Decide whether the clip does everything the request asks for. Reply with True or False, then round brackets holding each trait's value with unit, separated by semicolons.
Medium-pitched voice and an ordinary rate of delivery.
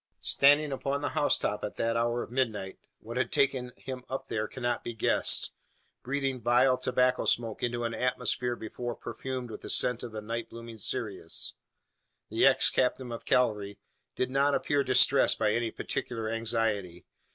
False (120 Hz; 165 wpm)